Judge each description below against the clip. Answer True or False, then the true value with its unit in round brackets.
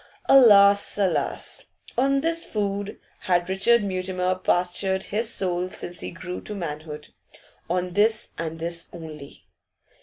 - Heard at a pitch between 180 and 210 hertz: True (185 Hz)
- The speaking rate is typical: False (125 wpm)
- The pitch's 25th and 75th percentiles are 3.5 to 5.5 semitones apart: False (2.9 semitones)